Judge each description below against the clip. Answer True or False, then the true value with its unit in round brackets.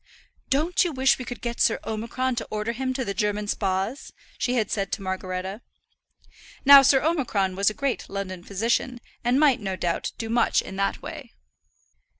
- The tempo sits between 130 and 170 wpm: False (180 wpm)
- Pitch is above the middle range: True (225 Hz)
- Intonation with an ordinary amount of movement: True (4.8 semitones)